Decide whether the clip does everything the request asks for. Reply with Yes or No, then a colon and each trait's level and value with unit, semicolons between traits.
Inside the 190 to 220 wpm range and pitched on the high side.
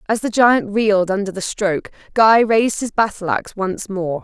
Yes: average, 200 wpm; high, 205 Hz